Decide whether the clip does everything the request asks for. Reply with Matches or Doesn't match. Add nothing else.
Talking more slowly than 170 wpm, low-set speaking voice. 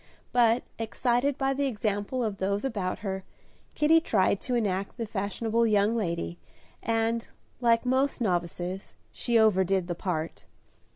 Doesn't match